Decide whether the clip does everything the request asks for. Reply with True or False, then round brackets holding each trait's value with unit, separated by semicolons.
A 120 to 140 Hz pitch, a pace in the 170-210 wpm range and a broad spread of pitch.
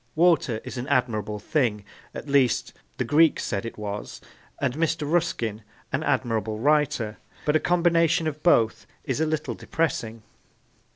False (135 Hz; 155 wpm; 6.0 semitones)